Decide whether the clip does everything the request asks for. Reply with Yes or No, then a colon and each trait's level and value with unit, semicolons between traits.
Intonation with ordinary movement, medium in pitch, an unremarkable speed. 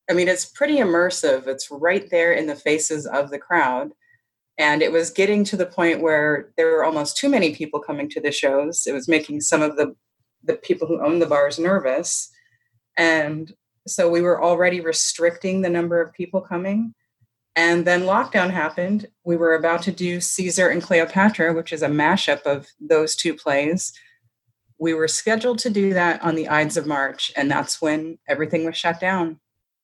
Yes: average, 3.1 semitones; medium, 165 Hz; average, 190 wpm